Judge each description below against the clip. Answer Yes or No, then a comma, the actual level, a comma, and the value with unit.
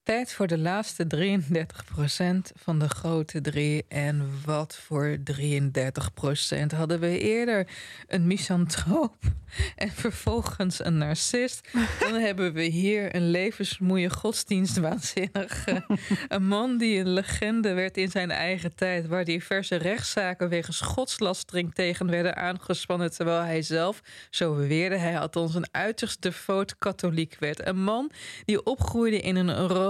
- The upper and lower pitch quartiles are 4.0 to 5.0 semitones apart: No, average, 3.0 semitones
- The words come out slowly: Yes, slow, 130 wpm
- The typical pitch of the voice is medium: Yes, medium, 180 Hz